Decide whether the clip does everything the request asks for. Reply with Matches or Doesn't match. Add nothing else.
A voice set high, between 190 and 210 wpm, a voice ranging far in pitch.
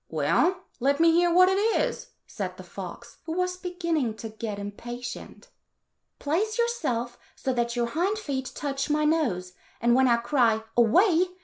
Doesn't match